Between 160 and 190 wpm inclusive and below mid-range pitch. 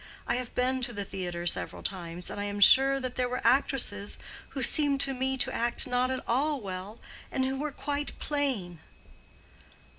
No: average, 180 wpm; very high, 250 Hz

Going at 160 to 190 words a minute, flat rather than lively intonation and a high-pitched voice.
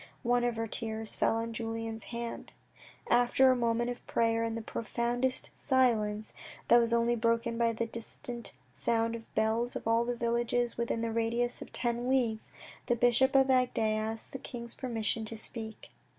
Yes: average, 180 wpm; narrow, 1.1 semitones; high, 235 Hz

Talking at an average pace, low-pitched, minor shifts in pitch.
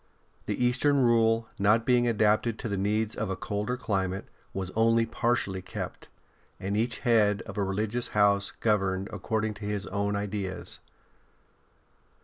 Yes: average, 145 wpm; low, 105 Hz; narrow, 2.3 semitones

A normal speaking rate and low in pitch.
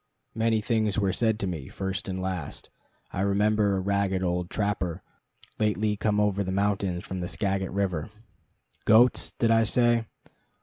Yes: average, 160 wpm; low, 100 Hz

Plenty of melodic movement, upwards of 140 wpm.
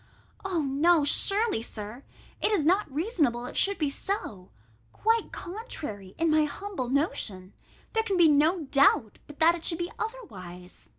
Yes: wide, 7.7 semitones; average, 155 wpm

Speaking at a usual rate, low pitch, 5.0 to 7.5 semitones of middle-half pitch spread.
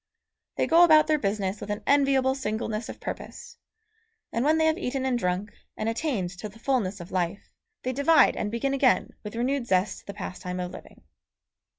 No: average, 190 wpm; high, 235 Hz; wide, 5.6 semitones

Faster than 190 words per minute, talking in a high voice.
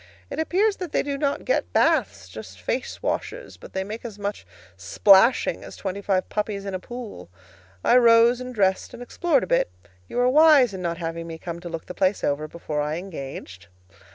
Yes: fast, 205 wpm; high, 195 Hz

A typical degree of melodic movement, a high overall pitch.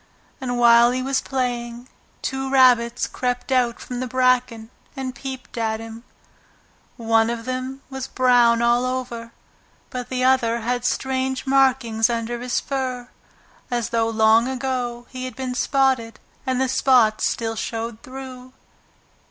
No: narrow, 1.8 semitones; high, 245 Hz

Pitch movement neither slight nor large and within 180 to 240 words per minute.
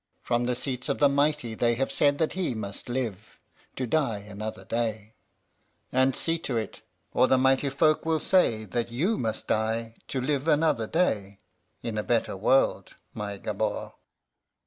No: average, 4.4 semitones; average, 170 wpm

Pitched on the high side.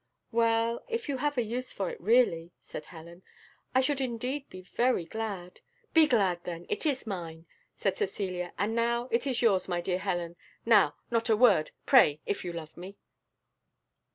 Yes: high, 220 Hz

